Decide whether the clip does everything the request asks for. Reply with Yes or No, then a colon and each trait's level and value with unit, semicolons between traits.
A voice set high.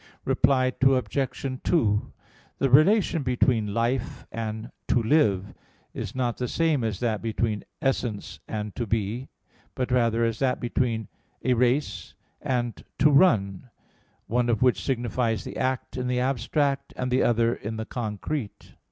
No: low, 120 Hz